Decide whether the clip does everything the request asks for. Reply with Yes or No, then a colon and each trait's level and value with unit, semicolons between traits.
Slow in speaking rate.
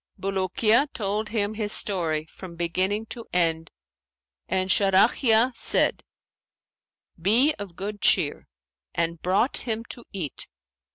Yes: slow, 115 wpm